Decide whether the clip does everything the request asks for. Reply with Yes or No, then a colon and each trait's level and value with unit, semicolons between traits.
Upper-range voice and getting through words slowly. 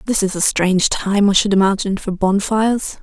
No: high, 200 Hz; average, 200 wpm